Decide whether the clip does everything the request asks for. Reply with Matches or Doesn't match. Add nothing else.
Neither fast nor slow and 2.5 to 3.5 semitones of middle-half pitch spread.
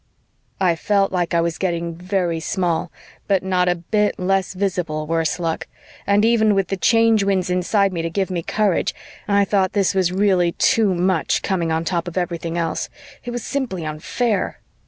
Matches